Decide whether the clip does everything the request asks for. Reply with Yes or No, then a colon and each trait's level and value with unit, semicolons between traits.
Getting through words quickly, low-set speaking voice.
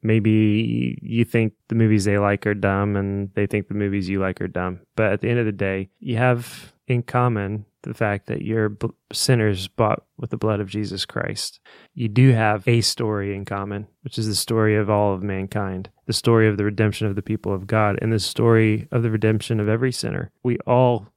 Yes: fast, 220 wpm; low, 105 Hz